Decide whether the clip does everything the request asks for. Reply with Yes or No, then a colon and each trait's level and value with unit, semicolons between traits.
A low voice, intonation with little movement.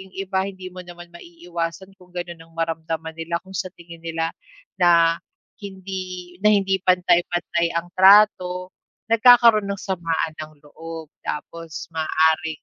No: medium, 175 Hz; narrow, 2.3 semitones